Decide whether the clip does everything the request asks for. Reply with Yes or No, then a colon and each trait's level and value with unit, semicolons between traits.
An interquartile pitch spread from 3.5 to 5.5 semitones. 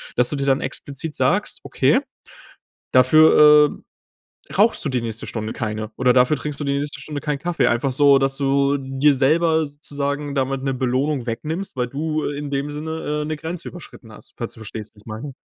No: average, 2.8 semitones